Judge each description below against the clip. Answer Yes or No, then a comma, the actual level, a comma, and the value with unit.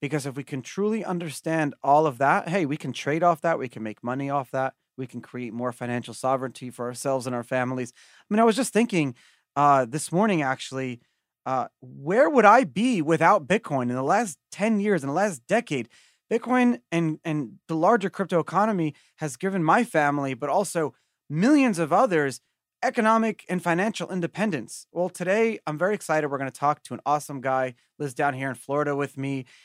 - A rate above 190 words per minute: Yes, average, 200 wpm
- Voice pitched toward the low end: No, medium, 150 Hz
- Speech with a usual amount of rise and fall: No, wide, 6.2 semitones